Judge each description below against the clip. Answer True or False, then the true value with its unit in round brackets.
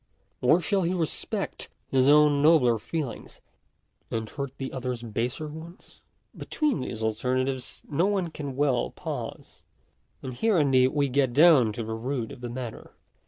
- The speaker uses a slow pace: False (160 wpm)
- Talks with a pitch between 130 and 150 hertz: True (135 Hz)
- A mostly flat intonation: False (4.2 semitones)